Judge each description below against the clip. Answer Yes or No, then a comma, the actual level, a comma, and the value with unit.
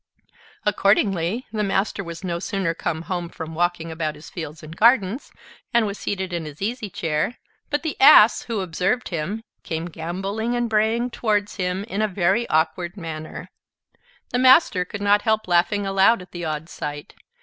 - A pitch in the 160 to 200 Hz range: Yes, high, 190 Hz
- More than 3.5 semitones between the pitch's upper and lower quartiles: Yes, average, 4.4 semitones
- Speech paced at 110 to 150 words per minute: No, average, 170 wpm